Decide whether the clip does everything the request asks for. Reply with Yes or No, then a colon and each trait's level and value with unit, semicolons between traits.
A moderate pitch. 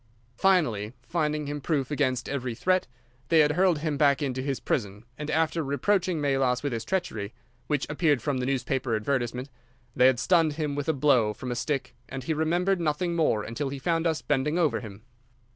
Yes: medium, 145 Hz